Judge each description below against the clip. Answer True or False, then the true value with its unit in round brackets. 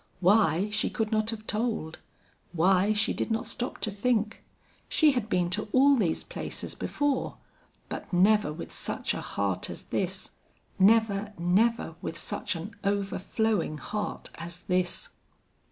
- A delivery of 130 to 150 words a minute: True (145 wpm)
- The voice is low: False (210 Hz)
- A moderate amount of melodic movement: True (3.6 semitones)